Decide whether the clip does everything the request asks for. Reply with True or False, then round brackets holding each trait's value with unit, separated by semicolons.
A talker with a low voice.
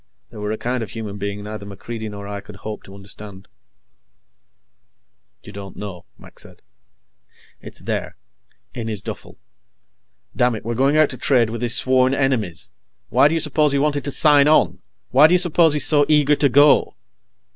True (120 Hz)